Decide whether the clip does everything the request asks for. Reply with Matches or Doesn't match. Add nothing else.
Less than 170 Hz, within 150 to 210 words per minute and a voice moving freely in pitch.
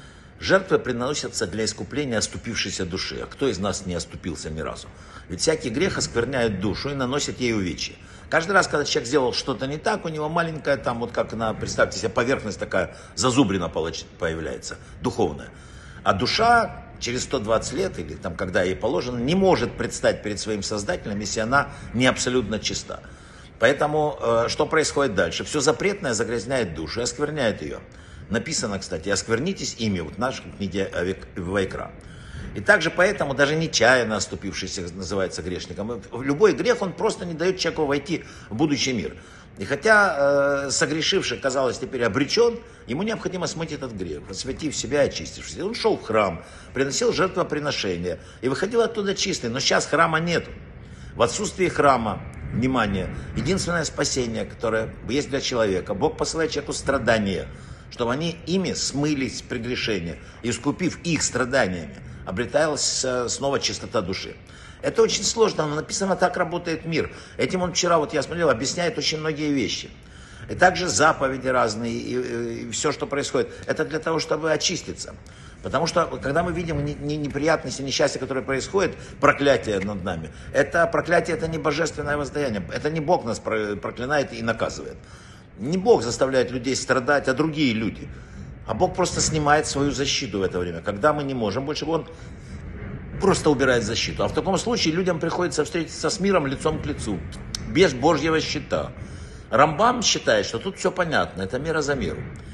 Matches